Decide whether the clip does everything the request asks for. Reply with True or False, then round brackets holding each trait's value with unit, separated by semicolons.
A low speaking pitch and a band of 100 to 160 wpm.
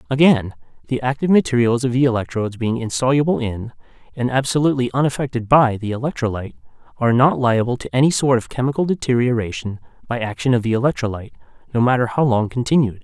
True (120 Hz; 155 wpm)